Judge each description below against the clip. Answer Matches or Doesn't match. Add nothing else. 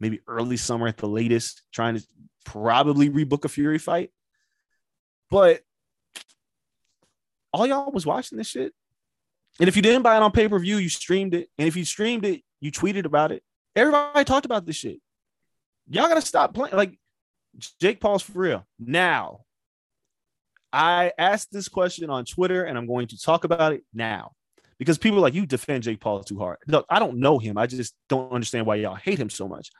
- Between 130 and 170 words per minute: Doesn't match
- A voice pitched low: Doesn't match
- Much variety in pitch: Matches